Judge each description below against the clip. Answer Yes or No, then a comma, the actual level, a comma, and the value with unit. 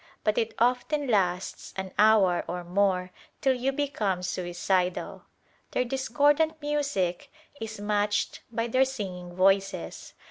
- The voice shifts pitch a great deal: Yes, wide, 6.0 semitones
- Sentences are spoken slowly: Yes, slow, 120 wpm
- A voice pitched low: No, high, 210 Hz